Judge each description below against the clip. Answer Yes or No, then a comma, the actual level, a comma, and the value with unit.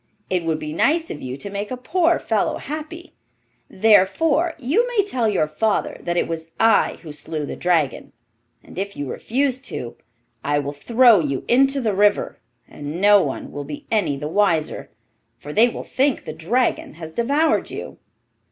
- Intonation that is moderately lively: No, wide, 8.8 semitones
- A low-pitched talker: No, high, 205 Hz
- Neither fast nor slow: Yes, average, 180 wpm